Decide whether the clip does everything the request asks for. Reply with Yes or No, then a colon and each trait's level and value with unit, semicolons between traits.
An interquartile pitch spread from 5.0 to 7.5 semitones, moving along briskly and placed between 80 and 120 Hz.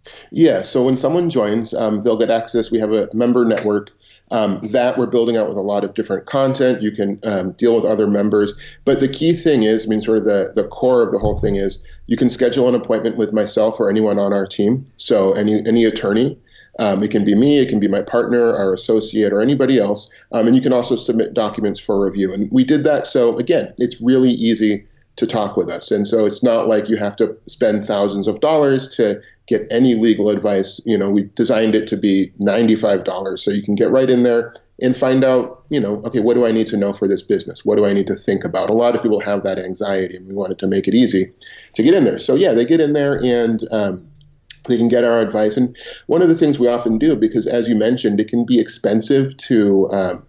No: average, 3.2 semitones; fast, 245 wpm; low, 110 Hz